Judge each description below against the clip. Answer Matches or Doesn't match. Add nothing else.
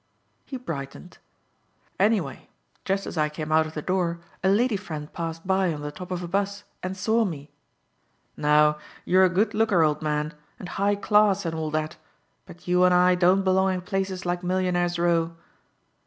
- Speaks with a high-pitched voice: Doesn't match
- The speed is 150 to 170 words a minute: Doesn't match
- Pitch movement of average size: Matches